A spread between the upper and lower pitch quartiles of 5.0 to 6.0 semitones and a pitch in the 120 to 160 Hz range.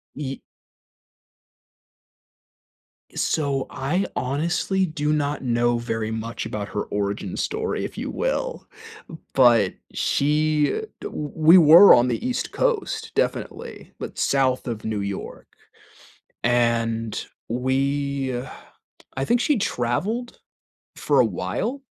Yes: wide, 5.5 semitones; low, 135 Hz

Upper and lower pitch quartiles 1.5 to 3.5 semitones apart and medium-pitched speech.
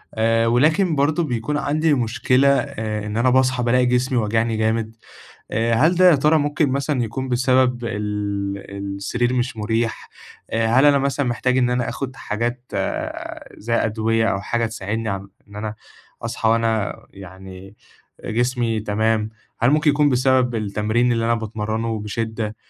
No: average, 3.0 semitones; low, 115 Hz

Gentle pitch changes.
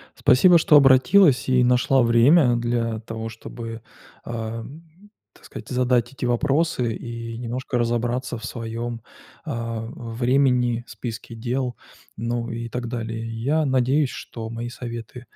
Yes: narrow, 2.0 semitones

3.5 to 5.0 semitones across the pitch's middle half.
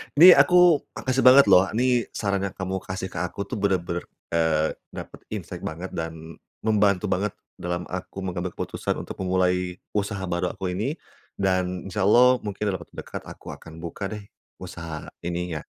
No: average, 2.8 semitones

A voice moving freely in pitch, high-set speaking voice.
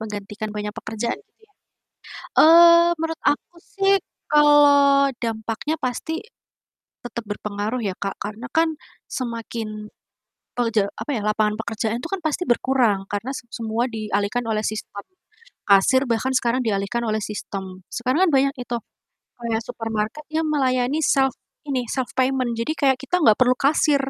No: average, 4.6 semitones; high, 240 Hz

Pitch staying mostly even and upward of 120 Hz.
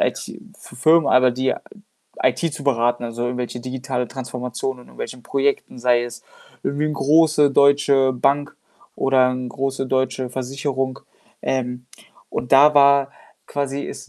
Yes: narrow, 2.0 semitones; low, 130 Hz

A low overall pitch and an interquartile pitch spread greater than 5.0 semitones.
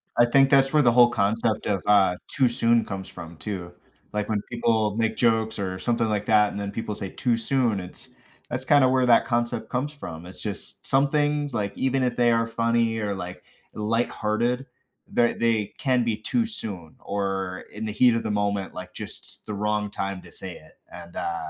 No: low, 110 Hz; average, 3.2 semitones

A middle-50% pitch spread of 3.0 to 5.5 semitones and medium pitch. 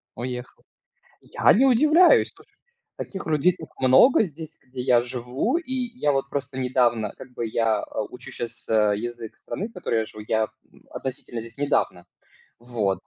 No: average, 4.8 semitones; low, 125 Hz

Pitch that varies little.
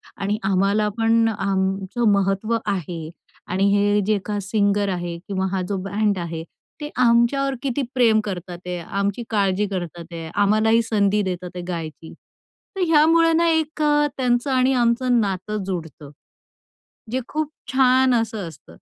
No: average, 4.3 semitones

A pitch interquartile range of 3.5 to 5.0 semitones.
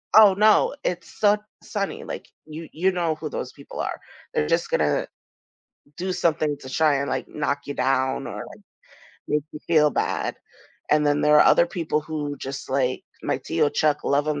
No: average, 2.9 semitones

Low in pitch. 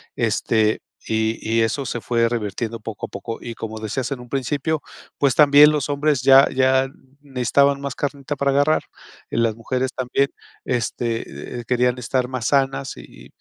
Yes: low, 125 Hz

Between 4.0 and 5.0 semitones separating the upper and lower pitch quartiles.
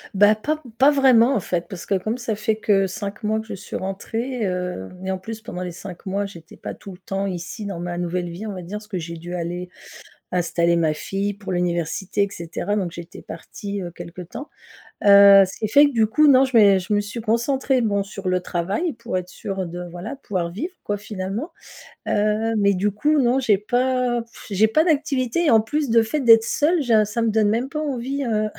Yes: average, 4.4 semitones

